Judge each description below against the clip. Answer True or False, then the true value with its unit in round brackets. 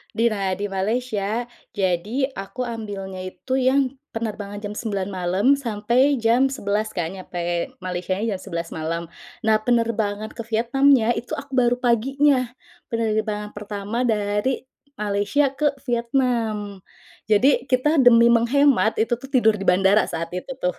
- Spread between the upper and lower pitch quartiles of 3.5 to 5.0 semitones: True (3.8 semitones)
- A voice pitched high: True (220 Hz)